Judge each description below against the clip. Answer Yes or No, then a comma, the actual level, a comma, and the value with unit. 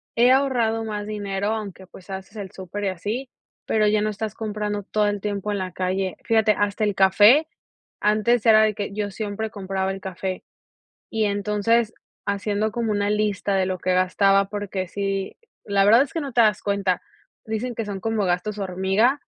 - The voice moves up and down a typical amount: No, narrow, 2.0 semitones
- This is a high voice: Yes, high, 205 Hz